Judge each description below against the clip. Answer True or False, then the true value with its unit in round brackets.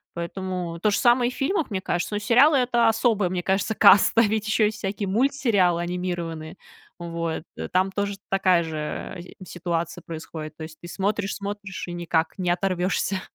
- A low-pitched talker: False (190 Hz)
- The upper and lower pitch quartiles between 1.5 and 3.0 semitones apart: False (3.6 semitones)